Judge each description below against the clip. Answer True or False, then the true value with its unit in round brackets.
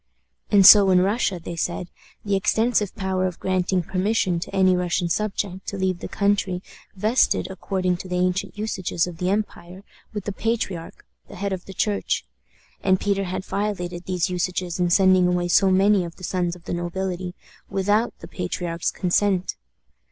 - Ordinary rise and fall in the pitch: False (1.9 semitones)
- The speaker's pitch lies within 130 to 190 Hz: True (185 Hz)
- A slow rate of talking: False (175 wpm)